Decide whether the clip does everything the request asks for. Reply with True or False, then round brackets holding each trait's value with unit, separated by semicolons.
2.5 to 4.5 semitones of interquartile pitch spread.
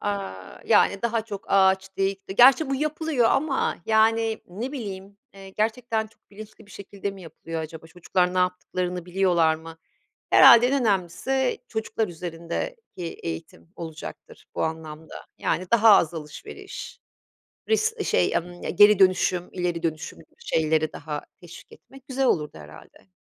False (5.2 semitones)